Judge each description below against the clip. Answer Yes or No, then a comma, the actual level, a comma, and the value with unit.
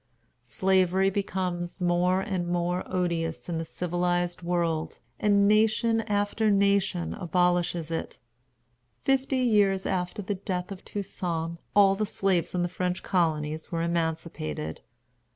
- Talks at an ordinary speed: No, slow, 125 wpm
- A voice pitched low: No, medium, 180 Hz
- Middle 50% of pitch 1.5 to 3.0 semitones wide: Yes, narrow, 2.6 semitones